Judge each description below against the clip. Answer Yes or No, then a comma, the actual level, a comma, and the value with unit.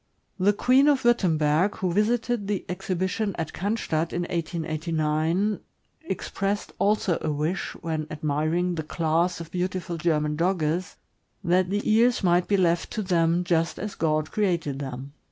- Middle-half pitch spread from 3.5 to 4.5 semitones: Yes, average, 3.8 semitones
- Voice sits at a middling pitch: Yes, medium, 175 Hz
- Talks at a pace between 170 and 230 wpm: No, average, 145 wpm